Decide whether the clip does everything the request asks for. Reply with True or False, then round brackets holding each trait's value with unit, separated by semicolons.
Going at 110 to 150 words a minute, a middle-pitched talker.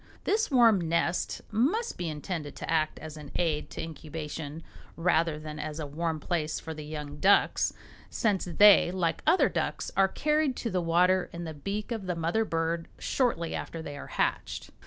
False (180 wpm; 165 Hz)